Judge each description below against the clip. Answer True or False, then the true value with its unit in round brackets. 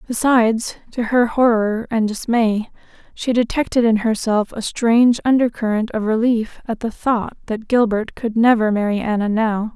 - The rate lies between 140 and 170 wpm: True (155 wpm)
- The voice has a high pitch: True (225 Hz)